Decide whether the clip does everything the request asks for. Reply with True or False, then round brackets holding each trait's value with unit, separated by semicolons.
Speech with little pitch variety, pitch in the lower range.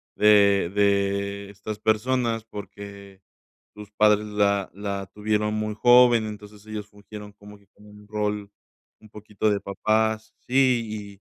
True (1.2 semitones; 105 Hz)